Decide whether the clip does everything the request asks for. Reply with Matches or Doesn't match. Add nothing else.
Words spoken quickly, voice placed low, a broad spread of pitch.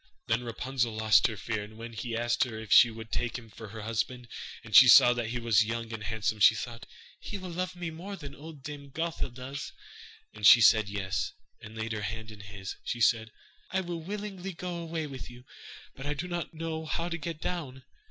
Matches